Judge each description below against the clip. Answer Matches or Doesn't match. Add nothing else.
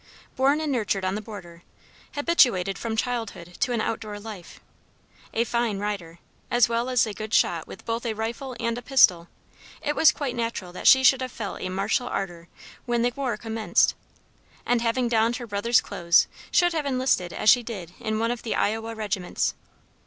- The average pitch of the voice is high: Matches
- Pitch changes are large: Doesn't match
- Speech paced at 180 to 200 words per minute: Matches